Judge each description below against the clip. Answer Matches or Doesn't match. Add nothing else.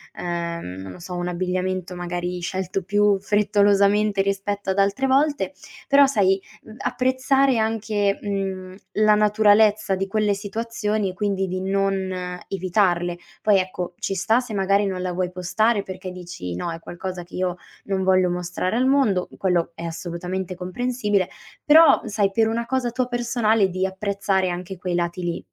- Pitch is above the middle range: Matches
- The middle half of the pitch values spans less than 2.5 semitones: Doesn't match